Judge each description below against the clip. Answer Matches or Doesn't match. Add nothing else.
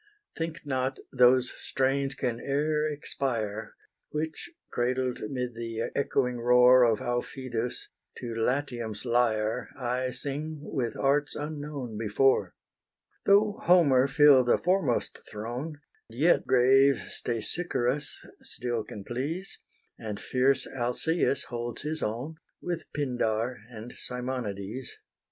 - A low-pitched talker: Matches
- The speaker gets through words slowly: Matches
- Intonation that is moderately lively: Matches